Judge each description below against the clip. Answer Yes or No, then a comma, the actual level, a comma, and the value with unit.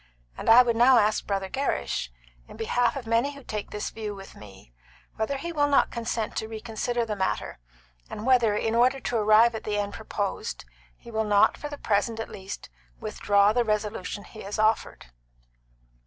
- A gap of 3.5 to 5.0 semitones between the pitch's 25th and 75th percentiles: No, narrow, 2.6 semitones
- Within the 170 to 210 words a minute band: Yes, average, 185 wpm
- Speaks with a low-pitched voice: No, high, 220 Hz